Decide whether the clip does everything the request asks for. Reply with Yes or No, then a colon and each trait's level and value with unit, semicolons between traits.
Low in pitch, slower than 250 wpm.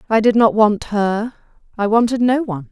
No: high, 220 Hz; average, 200 wpm